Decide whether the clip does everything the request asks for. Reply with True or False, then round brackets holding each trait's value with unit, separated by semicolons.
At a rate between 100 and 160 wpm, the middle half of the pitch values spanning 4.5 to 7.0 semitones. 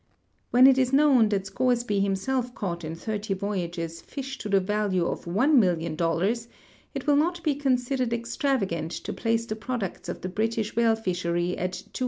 False (170 wpm; 5.4 semitones)